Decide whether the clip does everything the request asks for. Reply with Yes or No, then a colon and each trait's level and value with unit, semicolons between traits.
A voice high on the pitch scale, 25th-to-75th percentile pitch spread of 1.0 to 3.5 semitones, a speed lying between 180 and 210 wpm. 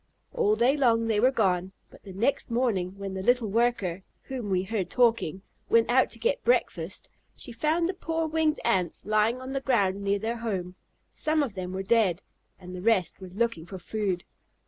No: high, 220 Hz; average, 4.8 semitones; average, 195 wpm